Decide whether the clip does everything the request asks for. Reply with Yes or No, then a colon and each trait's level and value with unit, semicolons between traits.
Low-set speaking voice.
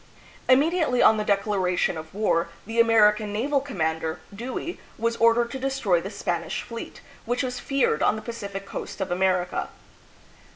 No: high, 215 Hz